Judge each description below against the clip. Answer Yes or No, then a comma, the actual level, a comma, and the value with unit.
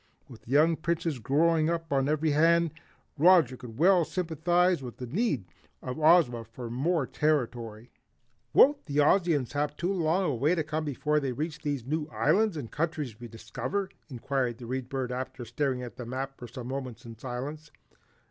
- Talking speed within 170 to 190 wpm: Yes, average, 175 wpm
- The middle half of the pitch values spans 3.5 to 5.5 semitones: Yes, average, 4.6 semitones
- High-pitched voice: No, medium, 145 Hz